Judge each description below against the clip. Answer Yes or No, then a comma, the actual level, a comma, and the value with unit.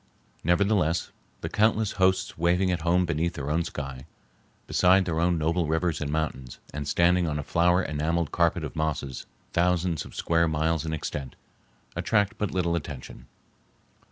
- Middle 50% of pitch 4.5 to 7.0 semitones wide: No, average, 2.7 semitones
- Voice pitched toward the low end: Yes, very low, 85 Hz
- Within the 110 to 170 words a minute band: Yes, average, 155 wpm